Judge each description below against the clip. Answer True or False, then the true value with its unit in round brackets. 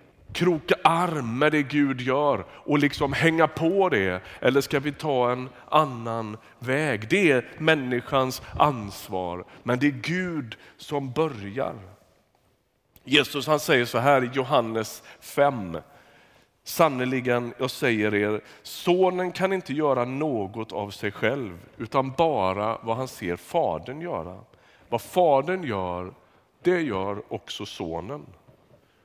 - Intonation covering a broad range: True (5.8 semitones)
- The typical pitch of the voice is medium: False (130 Hz)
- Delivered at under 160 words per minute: True (130 wpm)